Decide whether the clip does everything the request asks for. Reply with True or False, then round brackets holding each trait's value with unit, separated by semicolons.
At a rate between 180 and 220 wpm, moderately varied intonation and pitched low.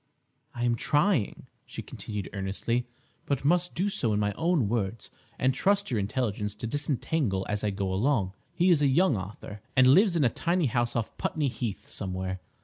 False (190 wpm; 6.4 semitones; 120 Hz)